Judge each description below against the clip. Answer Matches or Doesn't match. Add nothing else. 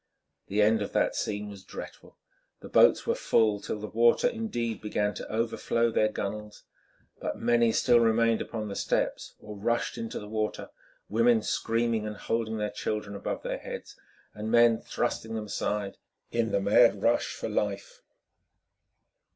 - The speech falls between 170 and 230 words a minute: Doesn't match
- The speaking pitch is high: Doesn't match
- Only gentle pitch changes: Matches